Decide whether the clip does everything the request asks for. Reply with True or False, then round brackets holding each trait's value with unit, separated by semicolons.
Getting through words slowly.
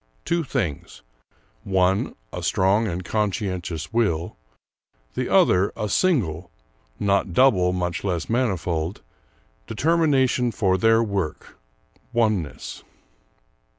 True (95 wpm)